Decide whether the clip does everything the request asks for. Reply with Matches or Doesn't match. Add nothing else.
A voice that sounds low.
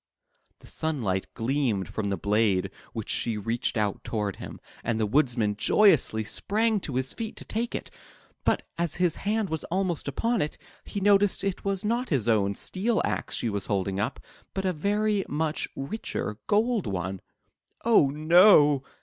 Doesn't match